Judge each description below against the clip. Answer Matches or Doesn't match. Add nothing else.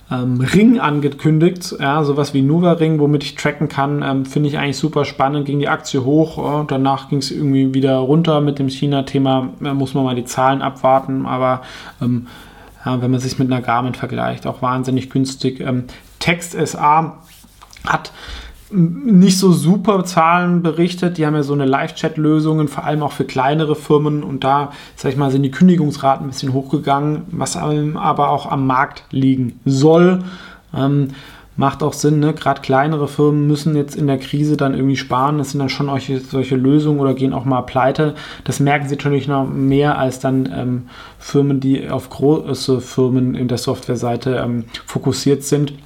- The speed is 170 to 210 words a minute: Matches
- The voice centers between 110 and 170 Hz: Matches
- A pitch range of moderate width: Doesn't match